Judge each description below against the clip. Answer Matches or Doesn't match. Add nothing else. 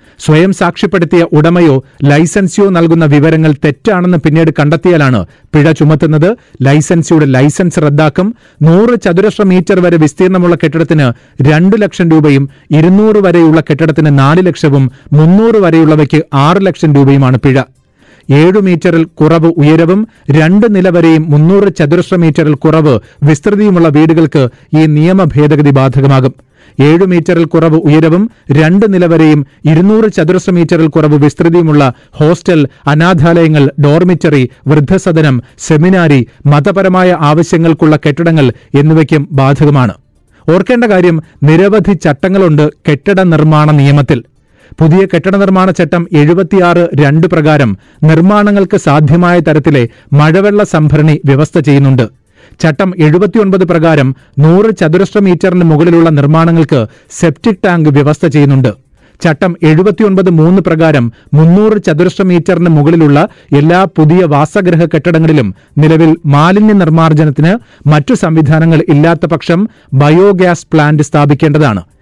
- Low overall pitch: Doesn't match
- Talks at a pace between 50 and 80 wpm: Doesn't match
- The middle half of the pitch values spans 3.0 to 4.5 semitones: Matches